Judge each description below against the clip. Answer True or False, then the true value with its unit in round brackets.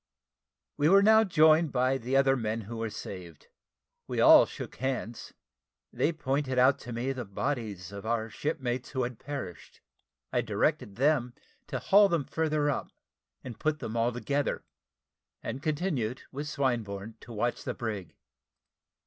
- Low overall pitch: True (130 Hz)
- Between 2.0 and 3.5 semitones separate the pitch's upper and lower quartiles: False (4.3 semitones)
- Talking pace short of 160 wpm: True (150 wpm)